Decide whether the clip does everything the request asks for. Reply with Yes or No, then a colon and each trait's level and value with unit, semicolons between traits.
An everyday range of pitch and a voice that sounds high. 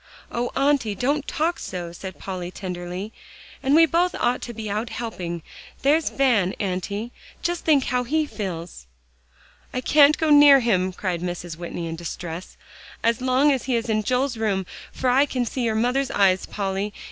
No: wide, 6.4 semitones; high, 230 Hz